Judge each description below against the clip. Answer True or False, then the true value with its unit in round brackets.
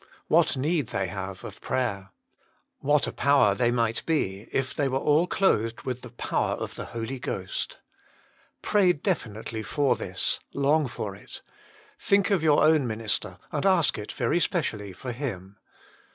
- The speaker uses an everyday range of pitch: False (6.0 semitones)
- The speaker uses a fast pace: False (160 wpm)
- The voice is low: True (125 Hz)